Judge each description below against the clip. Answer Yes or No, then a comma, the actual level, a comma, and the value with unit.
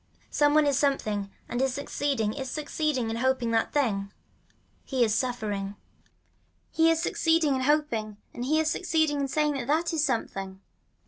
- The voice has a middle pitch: No, very high, 270 Hz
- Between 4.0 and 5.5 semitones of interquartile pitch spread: Yes, average, 4.9 semitones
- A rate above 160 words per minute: Yes, average, 170 wpm